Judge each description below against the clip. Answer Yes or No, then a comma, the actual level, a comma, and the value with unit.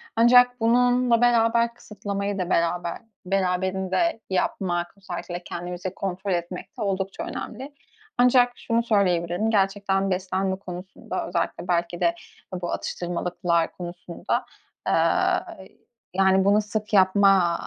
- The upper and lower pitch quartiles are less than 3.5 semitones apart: No, average, 3.8 semitones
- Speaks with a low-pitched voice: No, high, 190 Hz